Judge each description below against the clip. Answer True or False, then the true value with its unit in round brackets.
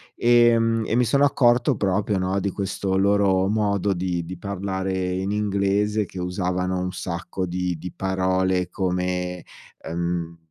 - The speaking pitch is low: True (95 Hz)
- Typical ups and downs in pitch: False (2.1 semitones)